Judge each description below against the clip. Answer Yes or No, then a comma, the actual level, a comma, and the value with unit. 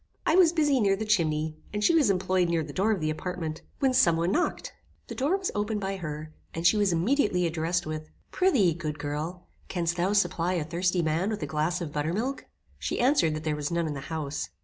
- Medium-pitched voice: Yes, medium, 175 Hz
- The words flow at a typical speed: No, fast, 225 wpm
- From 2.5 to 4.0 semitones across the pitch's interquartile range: No, average, 4.9 semitones